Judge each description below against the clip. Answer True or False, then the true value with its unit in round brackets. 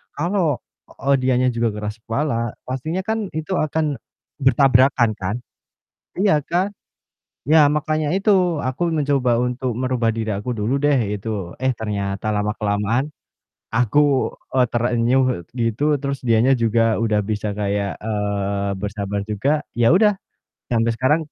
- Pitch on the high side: False (120 Hz)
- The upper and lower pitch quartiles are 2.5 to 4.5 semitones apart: False (4.9 semitones)